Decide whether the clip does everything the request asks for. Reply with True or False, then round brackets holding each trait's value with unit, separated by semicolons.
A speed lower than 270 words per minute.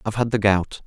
False (280 wpm)